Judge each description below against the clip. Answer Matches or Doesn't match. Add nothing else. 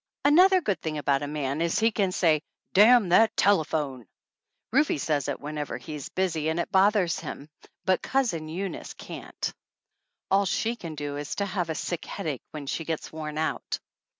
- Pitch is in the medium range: Matches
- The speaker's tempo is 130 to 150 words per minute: Doesn't match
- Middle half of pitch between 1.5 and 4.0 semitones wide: Doesn't match